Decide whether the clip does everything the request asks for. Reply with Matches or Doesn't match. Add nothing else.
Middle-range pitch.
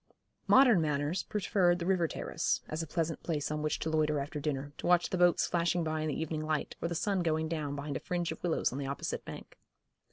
Matches